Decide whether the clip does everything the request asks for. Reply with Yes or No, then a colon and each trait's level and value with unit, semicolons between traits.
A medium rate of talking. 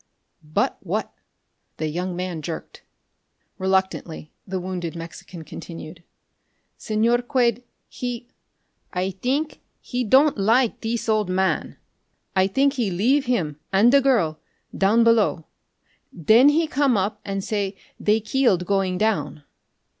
No: slow, 125 wpm